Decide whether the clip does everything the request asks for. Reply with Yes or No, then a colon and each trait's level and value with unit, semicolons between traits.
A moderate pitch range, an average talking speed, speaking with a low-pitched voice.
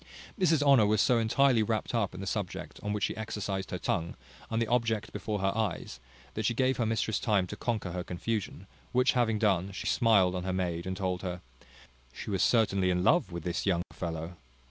No: average, 3.7 semitones; fast, 210 wpm; low, 105 Hz